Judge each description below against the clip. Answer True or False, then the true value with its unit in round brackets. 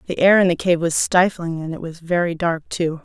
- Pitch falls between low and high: True (170 Hz)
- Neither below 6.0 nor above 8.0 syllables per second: False (5.3 syllables/s)